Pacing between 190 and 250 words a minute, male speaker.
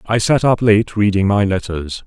Yes: fast, 205 wpm; male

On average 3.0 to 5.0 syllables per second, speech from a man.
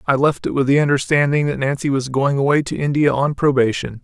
No: 5.9 syllables/s; male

